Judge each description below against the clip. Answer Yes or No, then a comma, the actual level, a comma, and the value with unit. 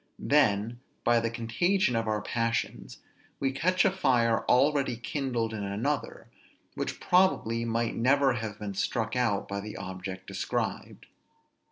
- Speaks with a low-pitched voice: Yes, low, 115 Hz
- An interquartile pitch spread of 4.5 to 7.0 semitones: No, average, 3.7 semitones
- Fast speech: No, average, 140 wpm